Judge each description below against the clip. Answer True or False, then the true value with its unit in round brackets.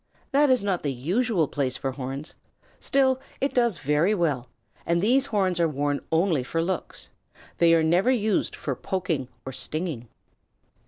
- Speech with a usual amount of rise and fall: False (6.5 semitones)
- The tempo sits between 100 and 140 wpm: False (160 wpm)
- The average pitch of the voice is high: False (170 Hz)